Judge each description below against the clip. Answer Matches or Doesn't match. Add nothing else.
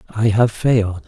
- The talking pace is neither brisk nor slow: Matches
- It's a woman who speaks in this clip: Doesn't match